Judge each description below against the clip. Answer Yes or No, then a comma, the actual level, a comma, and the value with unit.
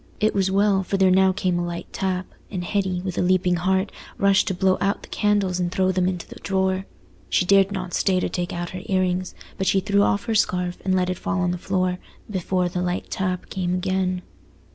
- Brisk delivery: Yes, fast, 230 wpm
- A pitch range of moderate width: No, narrow, 1.1 semitones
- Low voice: No, medium, 185 Hz